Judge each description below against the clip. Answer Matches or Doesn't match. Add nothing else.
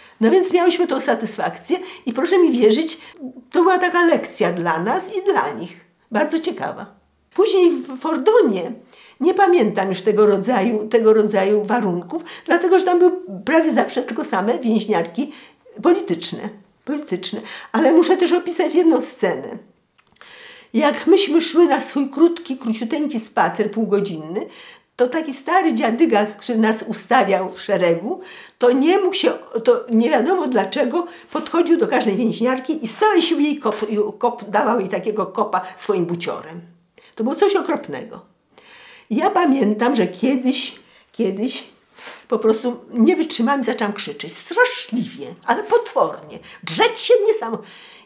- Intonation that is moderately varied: Doesn't match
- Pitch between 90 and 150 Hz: Doesn't match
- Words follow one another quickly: Doesn't match